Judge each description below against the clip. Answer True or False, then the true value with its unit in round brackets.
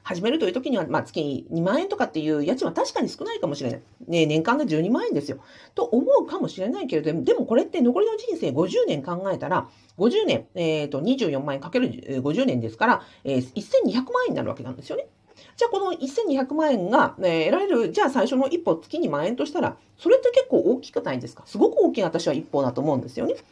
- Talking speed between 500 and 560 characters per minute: False (405 characters per minute)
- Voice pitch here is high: True (270 Hz)